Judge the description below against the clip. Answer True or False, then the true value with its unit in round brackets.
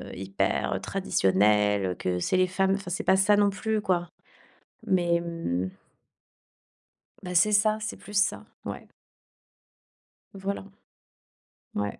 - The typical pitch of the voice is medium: True (180 Hz)